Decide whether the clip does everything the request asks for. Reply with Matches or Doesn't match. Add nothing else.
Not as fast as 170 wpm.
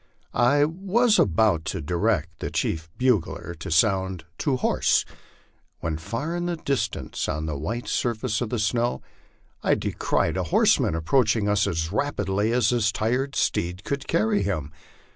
Matches